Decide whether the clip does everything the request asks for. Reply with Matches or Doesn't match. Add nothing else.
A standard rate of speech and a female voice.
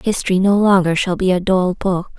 Doesn't match